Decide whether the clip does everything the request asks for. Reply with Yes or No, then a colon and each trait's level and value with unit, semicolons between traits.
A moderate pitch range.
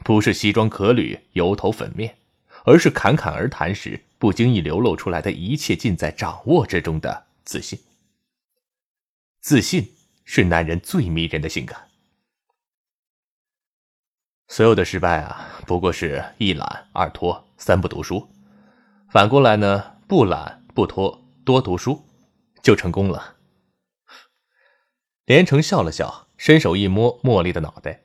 No: wide, 7.9 semitones